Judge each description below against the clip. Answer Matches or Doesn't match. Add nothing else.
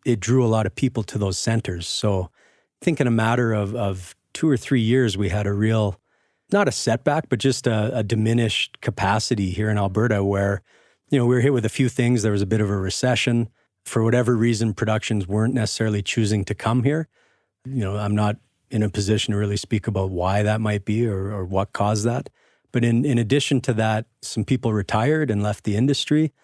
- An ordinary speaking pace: Doesn't match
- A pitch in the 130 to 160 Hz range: Doesn't match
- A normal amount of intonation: Matches